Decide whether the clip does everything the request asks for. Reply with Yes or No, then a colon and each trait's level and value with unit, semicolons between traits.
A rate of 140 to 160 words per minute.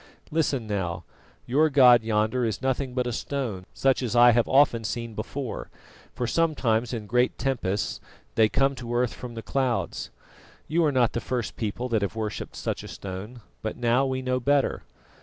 No: average, 180 wpm